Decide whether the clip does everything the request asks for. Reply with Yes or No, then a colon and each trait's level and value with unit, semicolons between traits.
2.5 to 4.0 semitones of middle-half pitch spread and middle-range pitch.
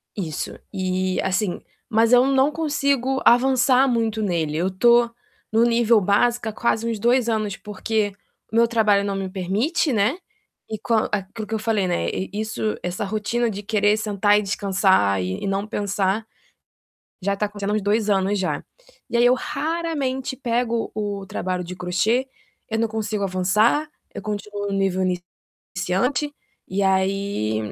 No: average, 3.4 semitones; high, 210 Hz